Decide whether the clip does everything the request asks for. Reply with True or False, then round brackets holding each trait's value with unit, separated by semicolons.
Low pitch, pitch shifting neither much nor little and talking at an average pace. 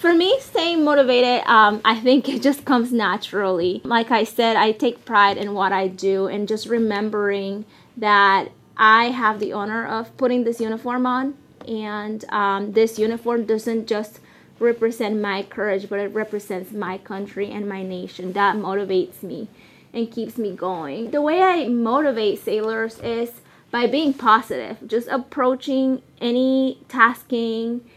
False (225 Hz; 3.2 semitones; 150 wpm)